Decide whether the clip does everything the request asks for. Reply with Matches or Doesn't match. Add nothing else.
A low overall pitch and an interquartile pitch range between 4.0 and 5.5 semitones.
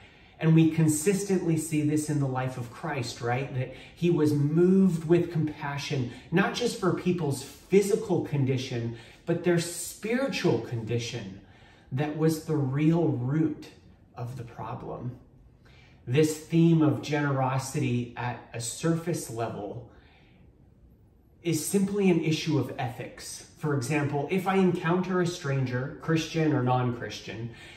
Doesn't match